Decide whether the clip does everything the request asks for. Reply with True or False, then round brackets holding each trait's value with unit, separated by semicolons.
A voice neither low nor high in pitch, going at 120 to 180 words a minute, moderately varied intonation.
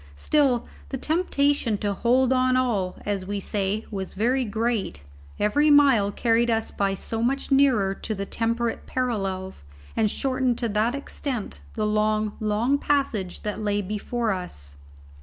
False (225 Hz; 150 wpm; 4.0 semitones)